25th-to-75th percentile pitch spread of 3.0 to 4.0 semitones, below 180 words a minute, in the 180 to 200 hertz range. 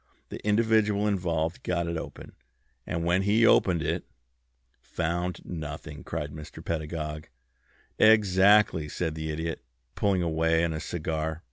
No: average, 3.4 semitones; slow, 135 wpm; very low, 85 Hz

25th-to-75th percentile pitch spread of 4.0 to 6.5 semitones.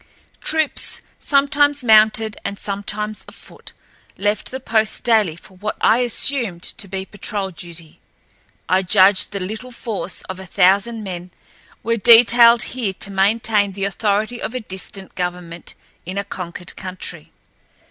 No: average, 3.3 semitones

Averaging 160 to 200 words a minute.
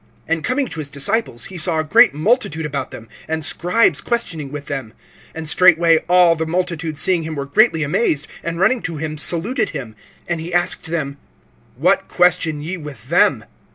Yes: average, 185 wpm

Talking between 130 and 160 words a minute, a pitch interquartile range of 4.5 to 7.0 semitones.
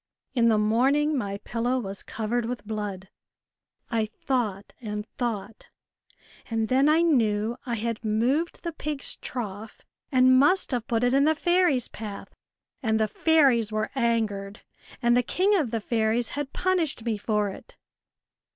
No: average, 155 wpm; average, 4.1 semitones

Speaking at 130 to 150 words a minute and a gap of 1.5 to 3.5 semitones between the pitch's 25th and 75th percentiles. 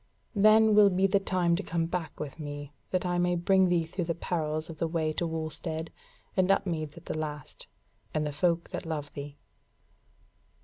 No: average, 190 wpm; average, 2.7 semitones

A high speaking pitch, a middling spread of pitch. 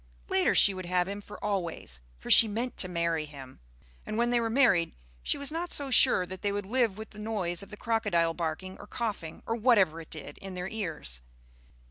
Yes: high, 195 Hz; average, 4.9 semitones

